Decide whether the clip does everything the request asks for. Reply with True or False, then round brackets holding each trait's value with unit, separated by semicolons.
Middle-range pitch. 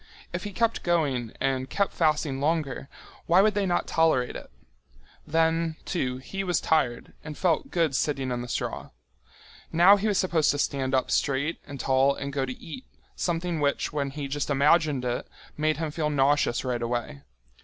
True (150 Hz)